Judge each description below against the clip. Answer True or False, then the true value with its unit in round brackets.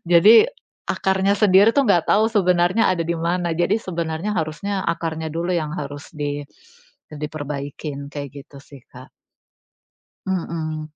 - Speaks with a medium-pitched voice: True (165 Hz)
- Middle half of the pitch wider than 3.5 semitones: True (4.1 semitones)